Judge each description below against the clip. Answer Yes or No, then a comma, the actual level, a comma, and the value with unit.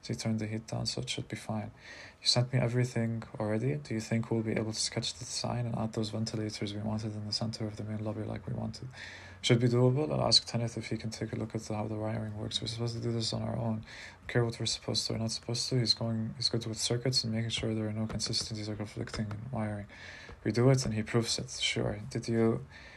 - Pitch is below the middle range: Yes, low, 110 Hz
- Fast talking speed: Yes, fast, 265 wpm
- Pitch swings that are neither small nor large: No, narrow, 1.4 semitones